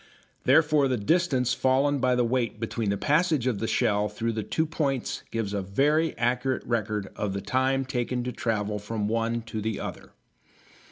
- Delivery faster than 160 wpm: Yes, average, 175 wpm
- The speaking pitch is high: No, low, 120 Hz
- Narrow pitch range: No, average, 3.9 semitones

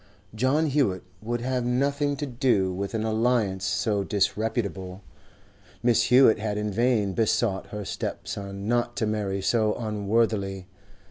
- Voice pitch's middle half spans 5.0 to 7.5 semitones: No, average, 3.4 semitones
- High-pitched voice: No, low, 110 Hz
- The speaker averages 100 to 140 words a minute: Yes, slow, 135 wpm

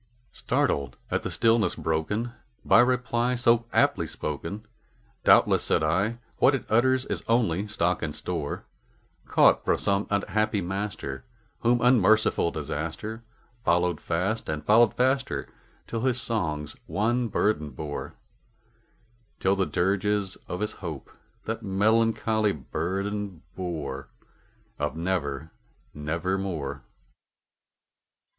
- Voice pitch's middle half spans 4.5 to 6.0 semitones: Yes, wide, 5.5 semitones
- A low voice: Yes, low, 100 Hz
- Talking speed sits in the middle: No, slow, 115 wpm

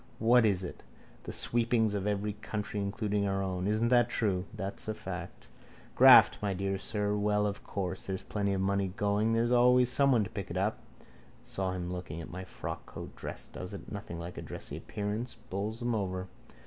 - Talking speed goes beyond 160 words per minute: Yes, average, 185 wpm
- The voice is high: No, low, 100 Hz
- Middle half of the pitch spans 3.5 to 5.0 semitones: No, narrow, 2.5 semitones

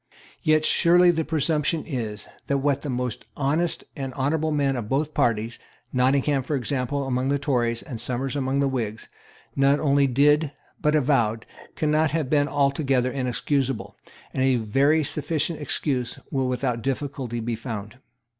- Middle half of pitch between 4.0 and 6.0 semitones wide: No, average, 2.9 semitones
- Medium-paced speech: Yes, average, 155 wpm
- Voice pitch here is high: No, low, 135 Hz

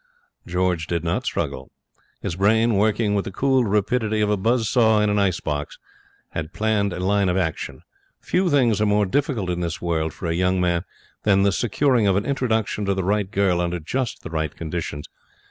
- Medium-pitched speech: No, low, 100 Hz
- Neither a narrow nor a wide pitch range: Yes, average, 3.9 semitones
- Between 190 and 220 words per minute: Yes, average, 200 wpm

